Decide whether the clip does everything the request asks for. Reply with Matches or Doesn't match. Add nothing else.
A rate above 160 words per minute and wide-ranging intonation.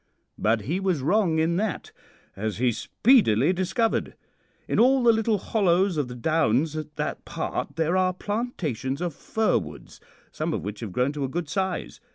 Matches